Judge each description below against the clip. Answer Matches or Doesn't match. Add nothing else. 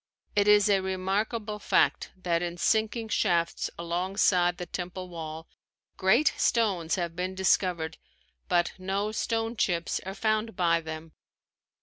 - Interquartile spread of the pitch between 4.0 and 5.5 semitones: Doesn't match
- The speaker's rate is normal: Doesn't match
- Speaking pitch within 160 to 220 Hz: Matches